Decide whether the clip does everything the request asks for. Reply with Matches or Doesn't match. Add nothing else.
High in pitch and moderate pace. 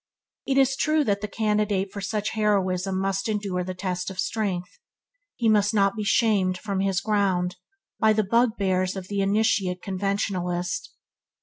Matches